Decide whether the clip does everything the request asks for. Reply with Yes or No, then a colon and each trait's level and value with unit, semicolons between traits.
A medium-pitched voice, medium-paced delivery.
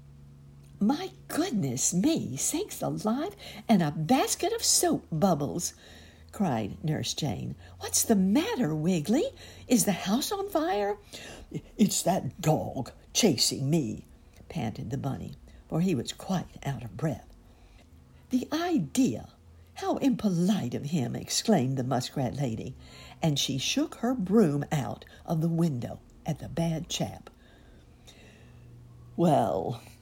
No: medium, 155 Hz; slow, 125 wpm